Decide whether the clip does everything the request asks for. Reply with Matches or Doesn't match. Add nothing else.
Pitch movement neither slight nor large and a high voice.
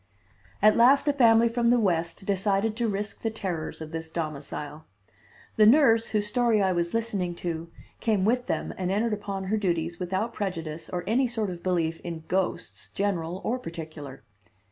Matches